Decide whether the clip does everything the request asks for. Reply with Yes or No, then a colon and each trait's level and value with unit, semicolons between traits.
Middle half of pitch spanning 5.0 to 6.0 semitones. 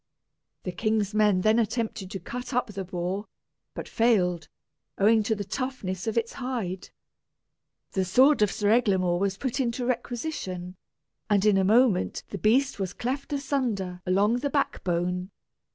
No: average, 4.6 semitones